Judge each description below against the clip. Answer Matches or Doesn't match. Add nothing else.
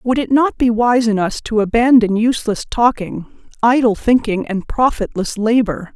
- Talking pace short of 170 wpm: Matches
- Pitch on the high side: Matches